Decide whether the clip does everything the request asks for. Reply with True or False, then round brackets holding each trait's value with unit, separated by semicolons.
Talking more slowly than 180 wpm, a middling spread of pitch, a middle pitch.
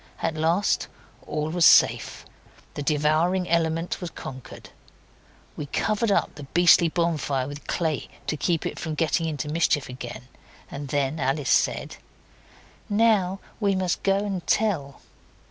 True (140 wpm; 3.7 semitones; 160 Hz)